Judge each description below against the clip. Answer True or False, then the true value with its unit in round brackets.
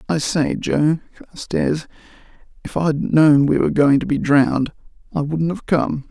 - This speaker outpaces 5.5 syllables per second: False (4.5 syllables/s)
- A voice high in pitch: False (155 Hz)